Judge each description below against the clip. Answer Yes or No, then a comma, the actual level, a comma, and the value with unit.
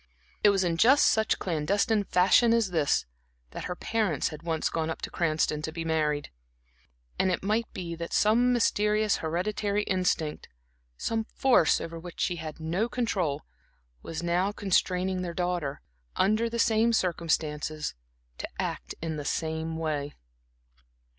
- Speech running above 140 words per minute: Yes, average, 150 wpm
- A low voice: No, medium, 175 Hz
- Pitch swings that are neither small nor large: Yes, average, 4.7 semitones